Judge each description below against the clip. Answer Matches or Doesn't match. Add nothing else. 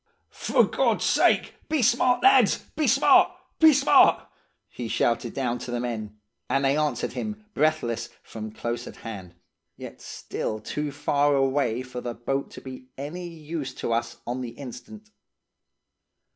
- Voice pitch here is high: Doesn't match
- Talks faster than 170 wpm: Doesn't match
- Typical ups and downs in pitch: Matches